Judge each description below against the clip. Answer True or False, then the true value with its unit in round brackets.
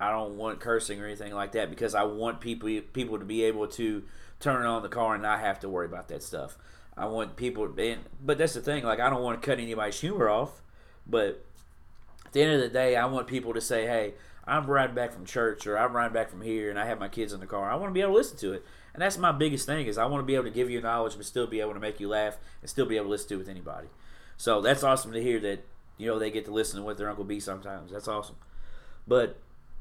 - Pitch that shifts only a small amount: False (3.2 semitones)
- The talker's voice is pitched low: True (110 Hz)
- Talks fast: True (285 wpm)